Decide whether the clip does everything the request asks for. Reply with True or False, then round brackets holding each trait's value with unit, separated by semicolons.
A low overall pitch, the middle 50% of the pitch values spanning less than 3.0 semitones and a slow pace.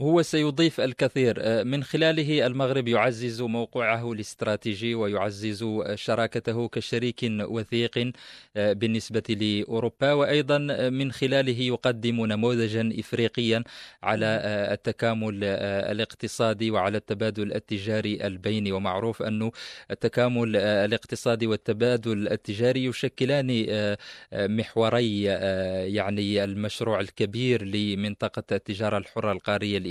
True (115 Hz; 2.5 semitones; 85 wpm)